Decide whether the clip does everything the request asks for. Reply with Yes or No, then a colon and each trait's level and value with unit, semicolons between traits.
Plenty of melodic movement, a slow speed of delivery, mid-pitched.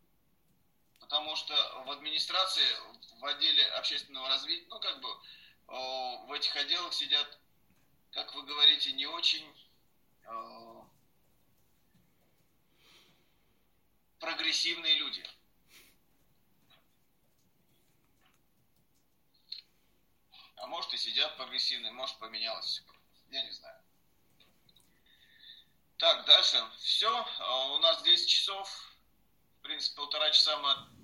Yes: wide, 5.7 semitones; slow, 90 wpm; medium, 155 Hz